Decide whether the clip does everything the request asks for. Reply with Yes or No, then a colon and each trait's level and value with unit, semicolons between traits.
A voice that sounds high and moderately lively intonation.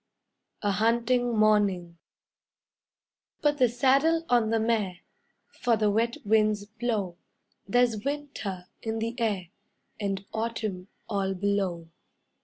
Yes: high, 220 Hz; average, 3.1 semitones